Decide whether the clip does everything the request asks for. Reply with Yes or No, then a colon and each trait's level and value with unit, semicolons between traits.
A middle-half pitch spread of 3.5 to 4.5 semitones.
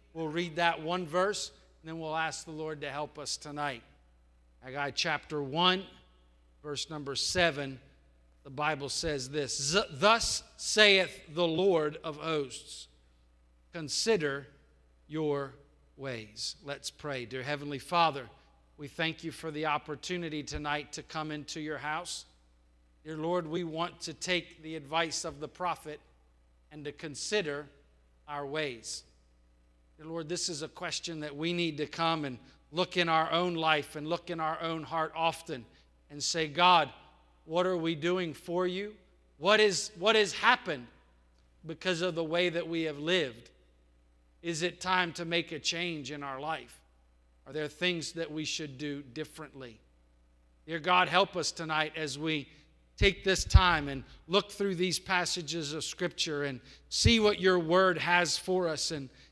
Yes: average, 4.0 semitones